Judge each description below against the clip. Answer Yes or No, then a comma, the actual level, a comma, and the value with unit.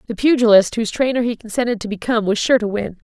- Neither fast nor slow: No, fast, 230 wpm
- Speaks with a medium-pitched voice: No, high, 225 Hz